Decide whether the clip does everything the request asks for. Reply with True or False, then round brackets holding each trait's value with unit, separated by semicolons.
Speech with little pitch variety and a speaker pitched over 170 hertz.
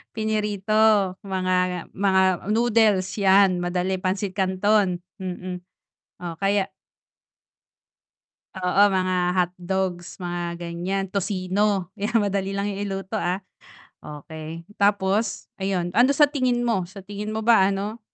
True (2.1 semitones; 190 Hz)